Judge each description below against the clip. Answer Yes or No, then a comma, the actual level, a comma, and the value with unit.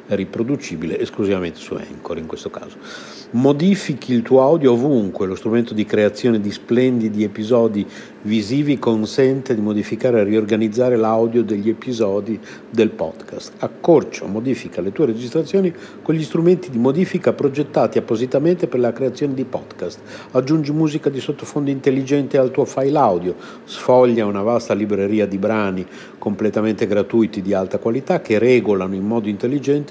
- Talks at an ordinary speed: Yes, average, 145 wpm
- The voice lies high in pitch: No, low, 120 Hz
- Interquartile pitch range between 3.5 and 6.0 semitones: Yes, average, 4.7 semitones